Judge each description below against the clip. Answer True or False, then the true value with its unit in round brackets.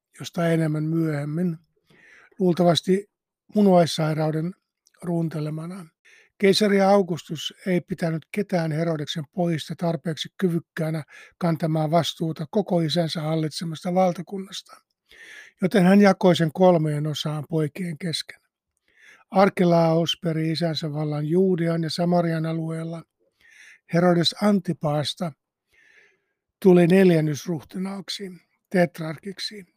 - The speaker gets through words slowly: True (85 wpm)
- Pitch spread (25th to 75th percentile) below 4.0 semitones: True (2.7 semitones)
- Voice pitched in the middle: True (170 Hz)